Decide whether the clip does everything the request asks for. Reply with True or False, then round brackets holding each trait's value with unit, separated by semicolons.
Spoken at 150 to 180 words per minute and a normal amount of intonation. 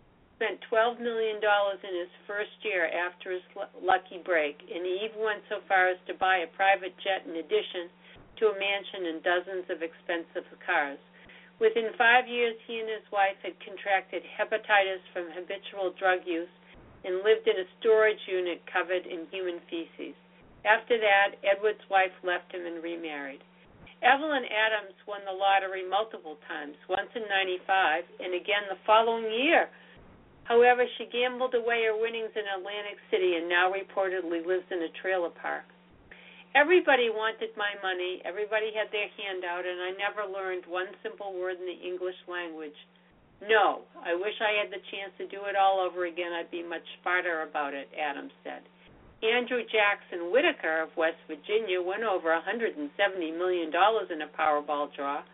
True (165 wpm; 3.2 semitones)